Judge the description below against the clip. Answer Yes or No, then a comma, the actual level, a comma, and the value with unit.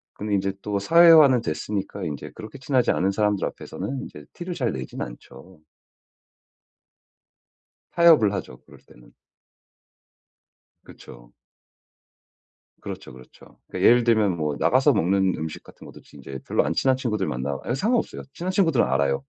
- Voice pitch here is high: No, low, 100 Hz